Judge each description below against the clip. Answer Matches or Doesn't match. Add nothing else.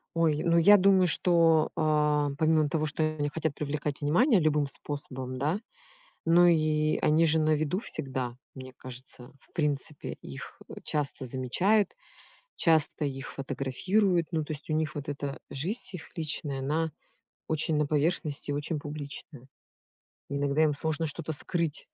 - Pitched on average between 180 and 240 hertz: Doesn't match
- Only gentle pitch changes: Matches